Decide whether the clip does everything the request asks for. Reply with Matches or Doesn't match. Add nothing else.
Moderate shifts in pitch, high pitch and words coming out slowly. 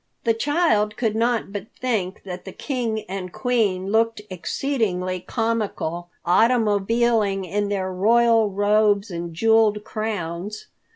Matches